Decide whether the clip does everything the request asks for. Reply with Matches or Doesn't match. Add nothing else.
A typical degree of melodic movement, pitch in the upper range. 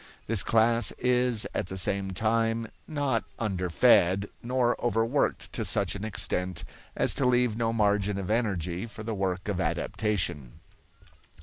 Doesn't match